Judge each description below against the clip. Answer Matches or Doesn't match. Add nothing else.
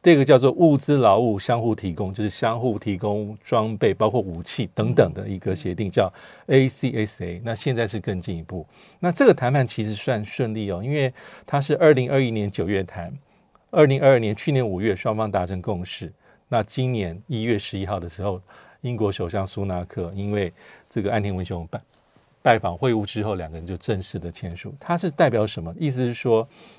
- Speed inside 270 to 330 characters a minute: Matches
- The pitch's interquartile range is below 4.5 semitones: Doesn't match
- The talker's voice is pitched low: Matches